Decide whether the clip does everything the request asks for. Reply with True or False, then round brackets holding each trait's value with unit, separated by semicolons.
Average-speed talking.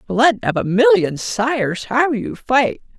True (160 wpm)